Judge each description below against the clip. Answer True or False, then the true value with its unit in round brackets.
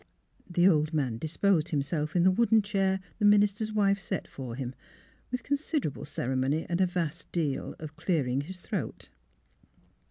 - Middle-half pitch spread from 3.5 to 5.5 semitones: True (5.0 semitones)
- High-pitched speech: False (175 Hz)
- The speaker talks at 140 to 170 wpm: True (160 wpm)